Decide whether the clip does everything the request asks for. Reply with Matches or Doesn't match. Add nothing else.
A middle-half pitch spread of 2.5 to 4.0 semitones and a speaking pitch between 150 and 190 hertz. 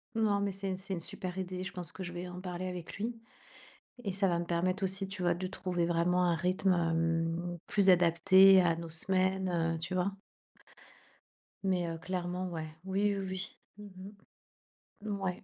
Doesn't match